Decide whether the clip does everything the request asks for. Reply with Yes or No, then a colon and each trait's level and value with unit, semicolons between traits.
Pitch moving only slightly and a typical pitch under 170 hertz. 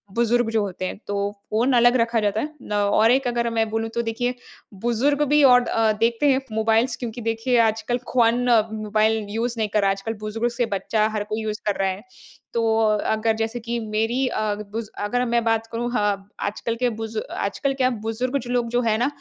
No: narrow, 2.1 semitones; high, 225 Hz